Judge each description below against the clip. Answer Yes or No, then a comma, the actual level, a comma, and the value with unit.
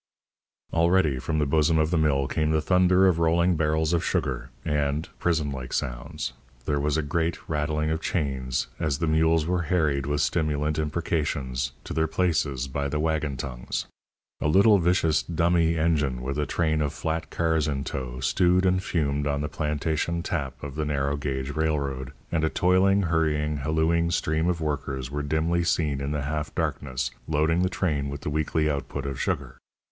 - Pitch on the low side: Yes, very low, 75 Hz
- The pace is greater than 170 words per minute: Yes, average, 180 wpm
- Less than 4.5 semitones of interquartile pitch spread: Yes, narrow, 2.6 semitones